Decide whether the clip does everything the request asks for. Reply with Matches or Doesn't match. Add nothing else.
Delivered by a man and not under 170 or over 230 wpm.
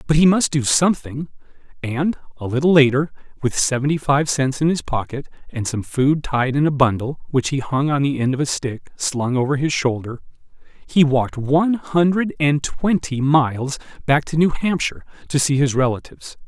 Matches